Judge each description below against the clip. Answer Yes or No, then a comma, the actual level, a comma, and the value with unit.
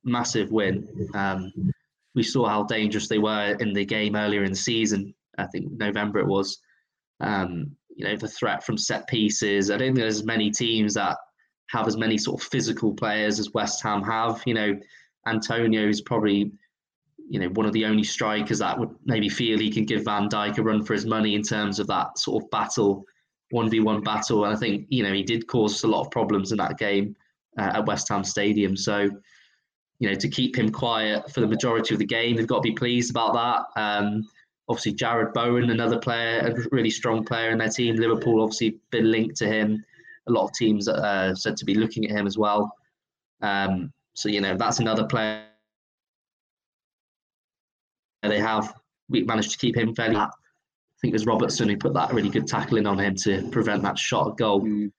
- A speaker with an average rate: No, fast, 210 wpm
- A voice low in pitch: Yes, low, 110 Hz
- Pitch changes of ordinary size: No, narrow, 1.7 semitones